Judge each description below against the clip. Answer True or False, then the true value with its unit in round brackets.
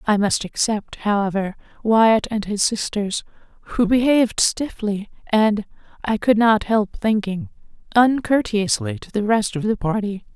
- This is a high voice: True (215 Hz)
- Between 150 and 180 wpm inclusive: False (140 wpm)